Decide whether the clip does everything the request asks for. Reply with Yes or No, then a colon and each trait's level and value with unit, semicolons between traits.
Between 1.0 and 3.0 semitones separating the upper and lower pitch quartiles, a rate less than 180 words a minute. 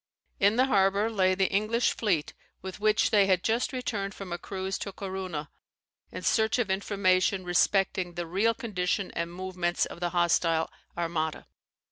Yes: average, 2.7 semitones; average, 160 wpm